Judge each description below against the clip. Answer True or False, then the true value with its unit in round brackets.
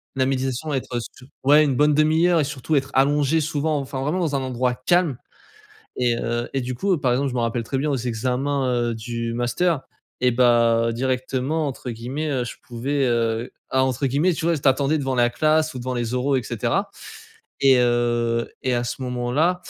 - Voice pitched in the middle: False (130 Hz)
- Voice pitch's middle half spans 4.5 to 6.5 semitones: False (3.3 semitones)